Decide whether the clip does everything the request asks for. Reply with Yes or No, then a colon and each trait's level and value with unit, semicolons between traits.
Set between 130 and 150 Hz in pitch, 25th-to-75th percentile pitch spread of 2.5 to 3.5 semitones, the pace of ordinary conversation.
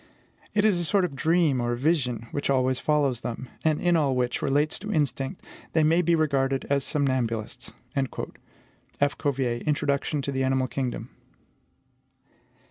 Yes: medium, 140 Hz; average, 3.2 semitones; average, 150 wpm